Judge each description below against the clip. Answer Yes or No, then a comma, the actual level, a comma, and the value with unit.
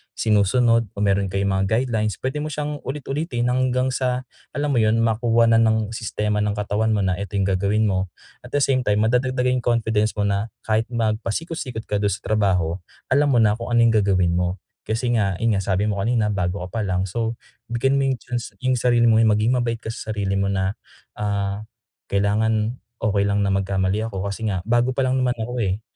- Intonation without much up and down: No, average, 3.3 semitones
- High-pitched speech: No, low, 110 Hz